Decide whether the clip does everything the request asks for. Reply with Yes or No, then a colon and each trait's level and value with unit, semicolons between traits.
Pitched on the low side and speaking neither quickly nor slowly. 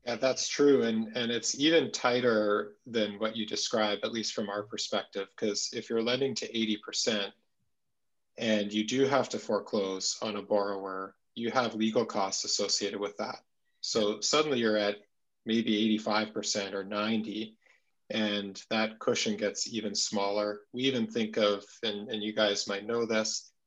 Yes: low, 110 Hz; average, 160 wpm